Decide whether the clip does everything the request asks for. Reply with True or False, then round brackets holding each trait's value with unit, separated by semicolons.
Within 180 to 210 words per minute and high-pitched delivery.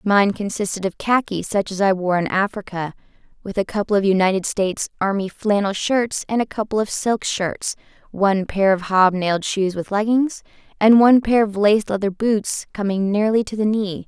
True (190 wpm; 205 Hz)